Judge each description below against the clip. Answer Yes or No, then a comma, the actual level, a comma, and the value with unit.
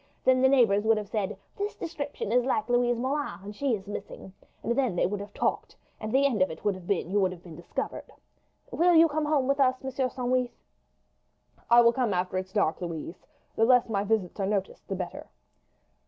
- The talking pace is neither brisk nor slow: No, fast, 215 wpm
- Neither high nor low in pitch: No, high, 225 Hz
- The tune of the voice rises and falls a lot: No, average, 5.0 semitones